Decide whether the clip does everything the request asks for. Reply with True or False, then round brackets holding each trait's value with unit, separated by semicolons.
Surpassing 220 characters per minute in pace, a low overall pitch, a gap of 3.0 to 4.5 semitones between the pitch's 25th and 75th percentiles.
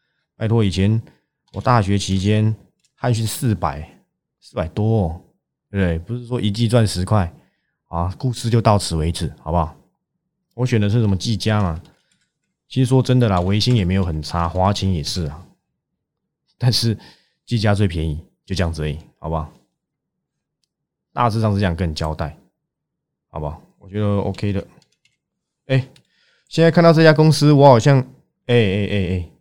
False (245 characters per minute; 105 Hz; 5.1 semitones)